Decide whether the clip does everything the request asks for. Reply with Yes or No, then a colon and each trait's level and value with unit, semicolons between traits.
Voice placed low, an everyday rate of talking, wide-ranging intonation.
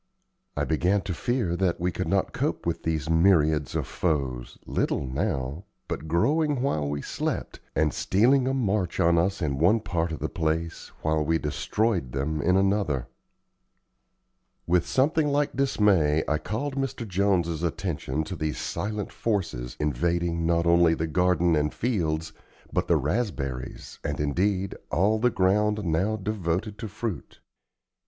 No: very low, 85 Hz; average, 150 wpm; average, 4.9 semitones